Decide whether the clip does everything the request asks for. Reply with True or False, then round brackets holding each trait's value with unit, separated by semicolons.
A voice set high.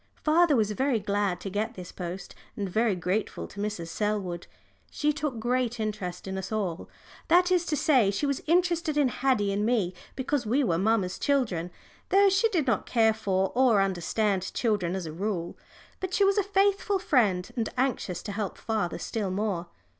True (220 Hz)